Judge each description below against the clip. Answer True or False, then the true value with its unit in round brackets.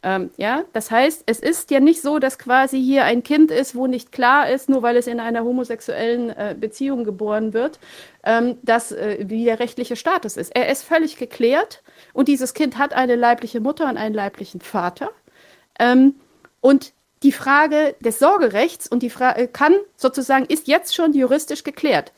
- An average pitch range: True (3.3 semitones)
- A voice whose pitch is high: True (255 Hz)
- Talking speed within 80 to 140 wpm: False (185 wpm)